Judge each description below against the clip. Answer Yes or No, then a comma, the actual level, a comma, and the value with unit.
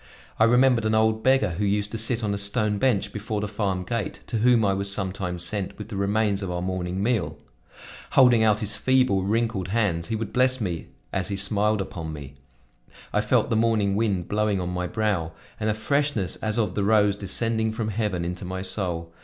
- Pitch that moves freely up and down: No, average, 2.8 semitones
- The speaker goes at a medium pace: No, fast, 210 wpm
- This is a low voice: Yes, low, 105 Hz